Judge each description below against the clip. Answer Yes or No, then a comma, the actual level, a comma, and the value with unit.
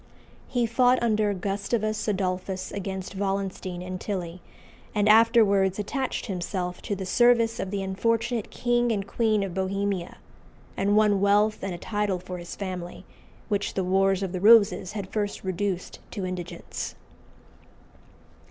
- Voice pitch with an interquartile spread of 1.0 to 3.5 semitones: Yes, narrow, 2.4 semitones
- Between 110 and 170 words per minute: Yes, average, 145 wpm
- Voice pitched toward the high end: Yes, high, 200 Hz